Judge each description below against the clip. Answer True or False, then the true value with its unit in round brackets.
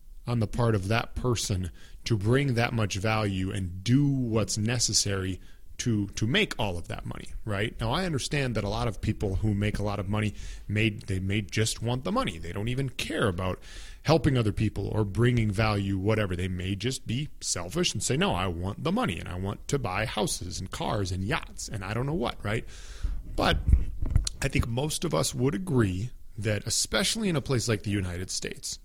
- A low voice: True (110 Hz)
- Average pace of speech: False (210 wpm)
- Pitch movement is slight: False (3.8 semitones)